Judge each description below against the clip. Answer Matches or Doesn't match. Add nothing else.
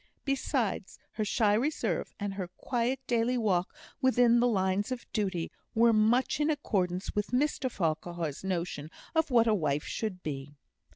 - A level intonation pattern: Doesn't match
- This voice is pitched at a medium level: Doesn't match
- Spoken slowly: Doesn't match